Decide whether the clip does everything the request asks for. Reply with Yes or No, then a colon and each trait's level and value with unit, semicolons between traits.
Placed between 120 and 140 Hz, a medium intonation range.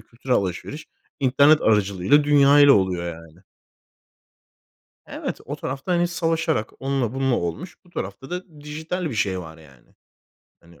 No: low, 135 Hz; wide, 8.1 semitones